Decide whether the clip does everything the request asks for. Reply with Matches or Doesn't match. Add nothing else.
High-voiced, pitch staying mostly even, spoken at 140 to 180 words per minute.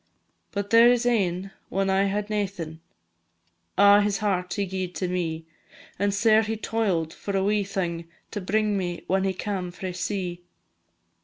Matches